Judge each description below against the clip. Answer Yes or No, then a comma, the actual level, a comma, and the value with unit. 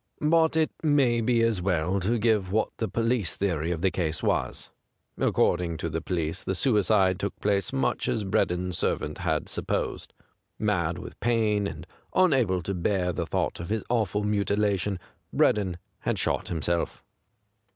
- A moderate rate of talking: Yes, average, 160 wpm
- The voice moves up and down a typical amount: Yes, average, 4.1 semitones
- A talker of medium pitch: No, low, 100 Hz